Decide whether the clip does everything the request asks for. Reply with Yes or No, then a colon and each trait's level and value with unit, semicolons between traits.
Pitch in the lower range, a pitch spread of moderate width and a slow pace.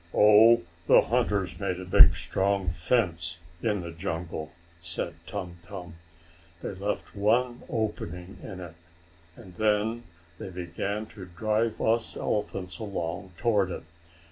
Yes: very low, 95 Hz; average, 3.5 semitones; slow, 130 wpm